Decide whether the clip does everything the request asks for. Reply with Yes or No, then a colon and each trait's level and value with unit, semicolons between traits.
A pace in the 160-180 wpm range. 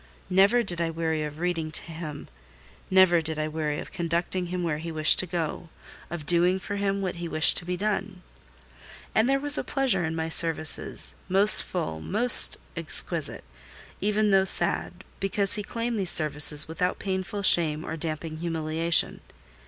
Yes: average, 170 wpm